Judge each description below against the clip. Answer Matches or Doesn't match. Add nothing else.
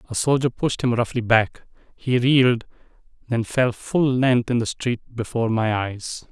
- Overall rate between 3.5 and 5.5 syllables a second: Matches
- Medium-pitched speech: Doesn't match